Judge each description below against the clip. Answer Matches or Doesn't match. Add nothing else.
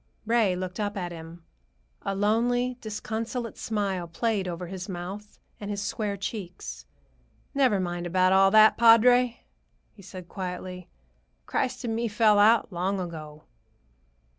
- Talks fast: Doesn't match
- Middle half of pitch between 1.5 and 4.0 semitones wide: Matches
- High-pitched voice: Matches